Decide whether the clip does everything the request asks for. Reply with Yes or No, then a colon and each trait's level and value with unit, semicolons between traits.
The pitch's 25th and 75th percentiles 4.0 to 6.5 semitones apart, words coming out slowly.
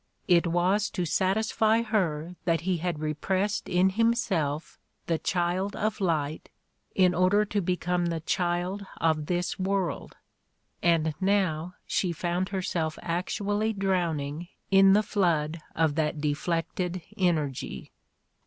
No: average, 3.0 semitones; slow, 125 wpm